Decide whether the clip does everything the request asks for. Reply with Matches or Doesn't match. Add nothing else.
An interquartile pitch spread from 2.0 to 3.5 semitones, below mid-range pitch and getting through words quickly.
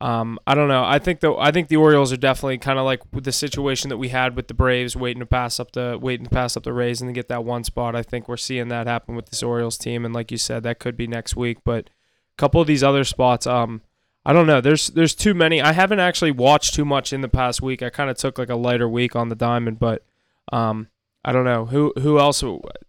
Matches